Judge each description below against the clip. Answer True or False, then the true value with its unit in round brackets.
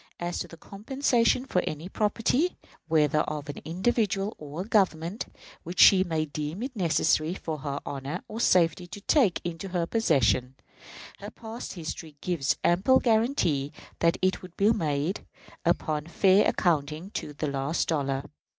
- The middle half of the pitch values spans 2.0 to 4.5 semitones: False (5.0 semitones)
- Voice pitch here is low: False (170 Hz)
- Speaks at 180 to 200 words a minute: False (155 wpm)